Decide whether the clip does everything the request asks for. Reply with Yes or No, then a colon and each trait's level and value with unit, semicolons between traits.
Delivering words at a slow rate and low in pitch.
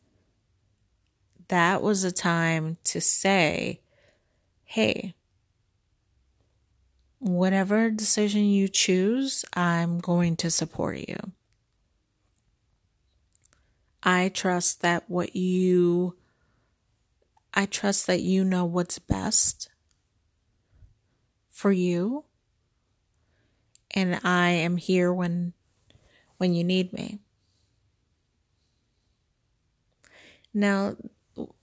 No: slow, 75 wpm; medium, 170 Hz